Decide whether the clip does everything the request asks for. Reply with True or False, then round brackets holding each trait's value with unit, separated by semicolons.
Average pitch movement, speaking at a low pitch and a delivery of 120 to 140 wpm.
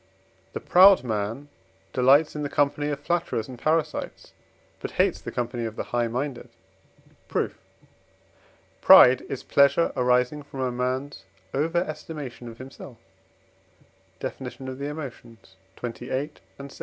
True (3.1 semitones; 130 Hz; 135 wpm)